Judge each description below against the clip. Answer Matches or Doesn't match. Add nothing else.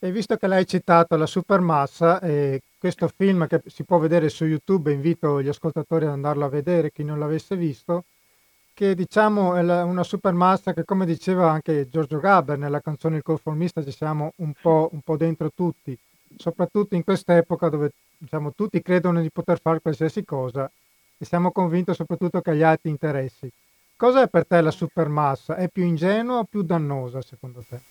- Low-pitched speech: Doesn't match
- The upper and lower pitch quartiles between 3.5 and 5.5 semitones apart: Doesn't match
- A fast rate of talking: Matches